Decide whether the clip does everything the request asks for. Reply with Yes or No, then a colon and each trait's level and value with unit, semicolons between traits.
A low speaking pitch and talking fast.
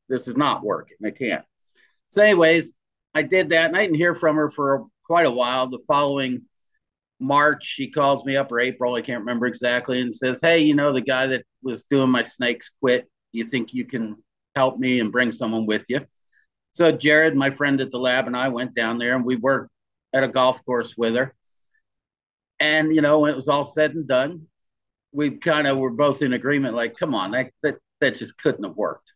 Yes: low, 130 Hz; fast, 220 wpm